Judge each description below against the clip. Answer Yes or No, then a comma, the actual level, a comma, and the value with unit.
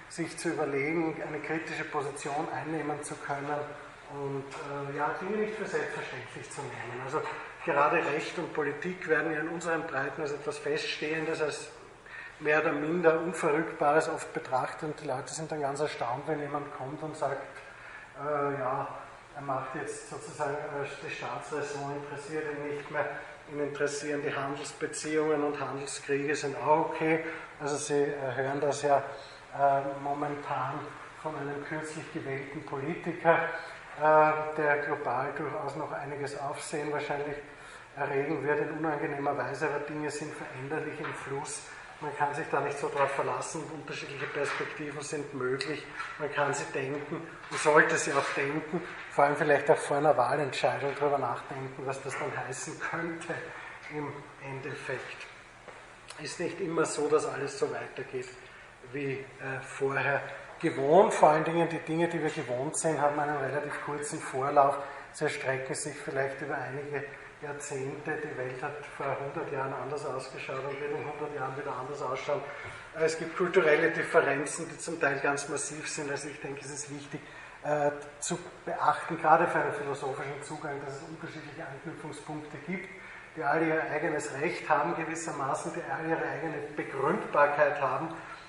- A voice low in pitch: No, medium, 145 Hz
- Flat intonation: Yes, narrow, 1.6 semitones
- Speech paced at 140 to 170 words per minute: Yes, average, 155 wpm